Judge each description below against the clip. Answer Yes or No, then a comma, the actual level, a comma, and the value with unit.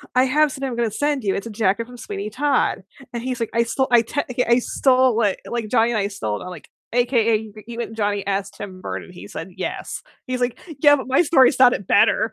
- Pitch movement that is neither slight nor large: Yes, average, 3.5 semitones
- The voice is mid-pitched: No, high, 235 Hz